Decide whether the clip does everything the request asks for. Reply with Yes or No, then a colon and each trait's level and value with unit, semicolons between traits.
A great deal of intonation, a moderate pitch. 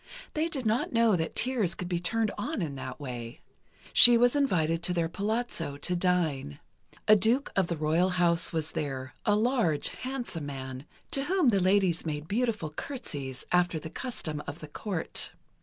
Yes: wide, 6.8 semitones; medium, 180 Hz